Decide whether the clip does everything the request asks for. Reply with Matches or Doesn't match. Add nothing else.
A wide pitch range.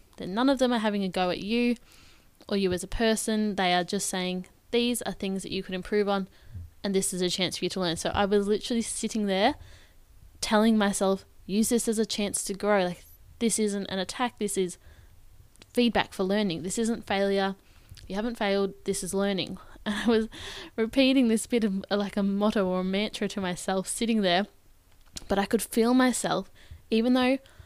Doesn't match